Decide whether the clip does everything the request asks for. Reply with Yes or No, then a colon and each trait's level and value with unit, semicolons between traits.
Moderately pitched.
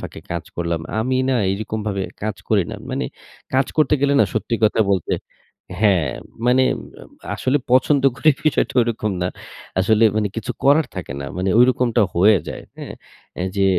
No: low, 110 Hz